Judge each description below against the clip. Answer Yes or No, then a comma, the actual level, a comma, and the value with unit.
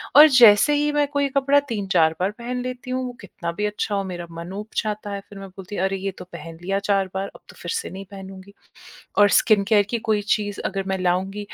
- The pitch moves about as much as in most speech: Yes, average, 3.5 semitones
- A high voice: Yes, high, 205 Hz